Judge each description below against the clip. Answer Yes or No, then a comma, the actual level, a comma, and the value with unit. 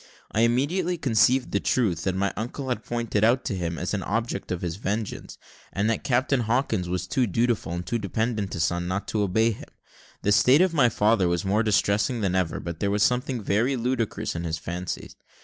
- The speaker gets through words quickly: Yes, fast, 215 wpm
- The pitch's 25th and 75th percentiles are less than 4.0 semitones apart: No, average, 4.7 semitones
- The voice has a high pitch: No, low, 105 Hz